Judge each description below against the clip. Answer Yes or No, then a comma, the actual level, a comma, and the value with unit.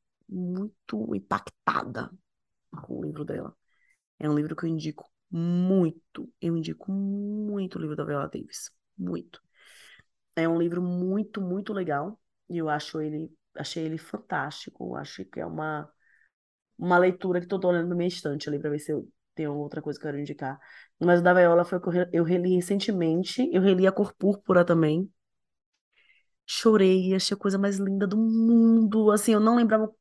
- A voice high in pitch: No, medium, 180 Hz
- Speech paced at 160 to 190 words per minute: Yes, average, 180 wpm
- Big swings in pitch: No, average, 4.3 semitones